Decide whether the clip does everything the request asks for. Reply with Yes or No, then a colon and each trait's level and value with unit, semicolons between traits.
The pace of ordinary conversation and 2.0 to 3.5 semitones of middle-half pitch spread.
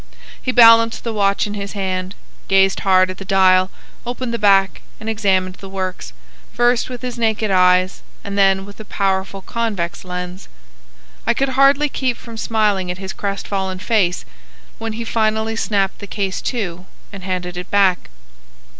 Yes: average, 165 wpm; average, 3.1 semitones